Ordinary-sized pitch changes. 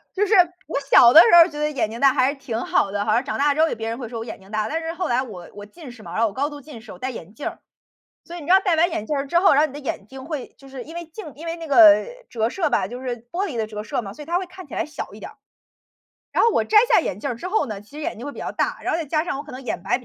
No: wide, 6.0 semitones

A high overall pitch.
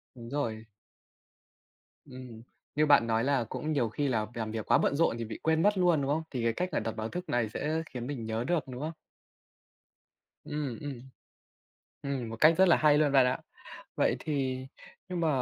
No: low, 135 Hz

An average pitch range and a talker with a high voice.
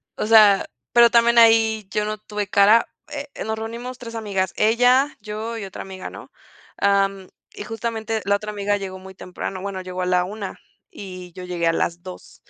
Yes: average, 3.0 semitones; high, 205 Hz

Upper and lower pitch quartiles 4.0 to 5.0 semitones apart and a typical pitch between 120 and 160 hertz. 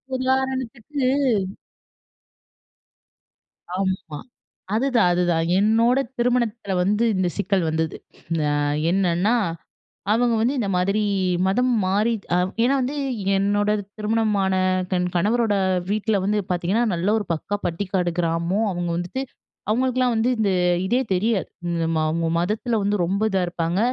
No: average, 4.6 semitones; high, 205 Hz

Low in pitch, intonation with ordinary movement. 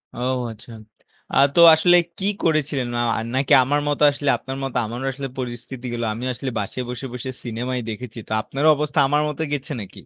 Yes: low, 130 Hz; average, 3.1 semitones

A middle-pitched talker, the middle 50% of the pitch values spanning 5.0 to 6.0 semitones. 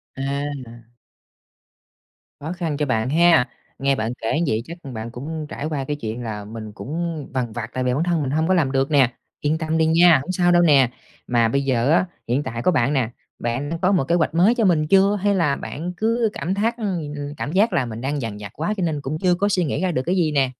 Yes: medium, 150 Hz; average, 5.3 semitones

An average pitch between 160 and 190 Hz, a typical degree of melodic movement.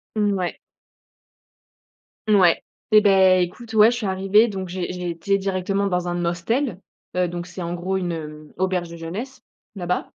No: medium, 185 Hz; narrow, 2.3 semitones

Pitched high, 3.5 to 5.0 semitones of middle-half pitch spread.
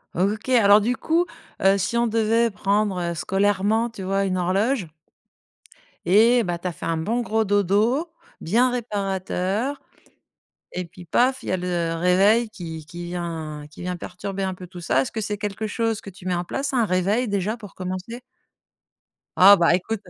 Yes: high, 195 Hz; average, 3.8 semitones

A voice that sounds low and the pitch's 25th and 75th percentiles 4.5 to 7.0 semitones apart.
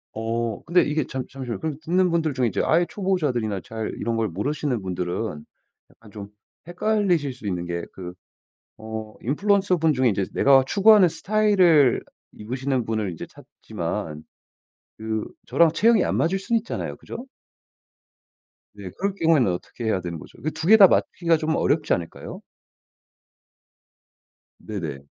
No: low, 130 Hz; wide, 8.1 semitones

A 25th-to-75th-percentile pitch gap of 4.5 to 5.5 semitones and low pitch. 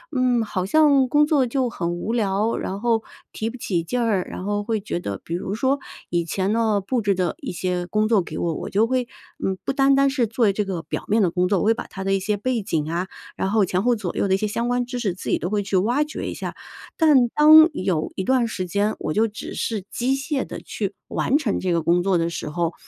No: average, 4.9 semitones; high, 210 Hz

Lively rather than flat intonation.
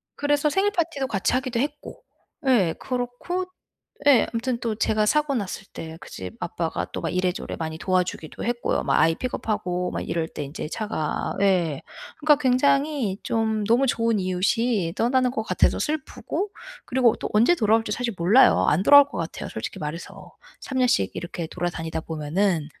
Yes: wide, 6.8 semitones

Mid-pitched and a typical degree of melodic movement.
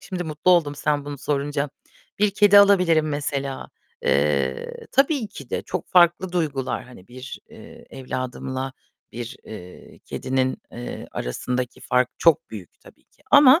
No: medium, 145 Hz; wide, 5.8 semitones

